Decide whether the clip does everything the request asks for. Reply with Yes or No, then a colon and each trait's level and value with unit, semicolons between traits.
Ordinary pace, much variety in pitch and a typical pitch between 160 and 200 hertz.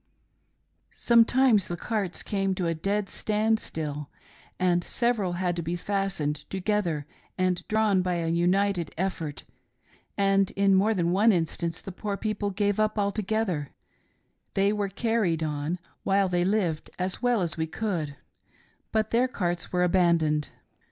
No: average, 150 wpm; average, 3.5 semitones; high, 190 Hz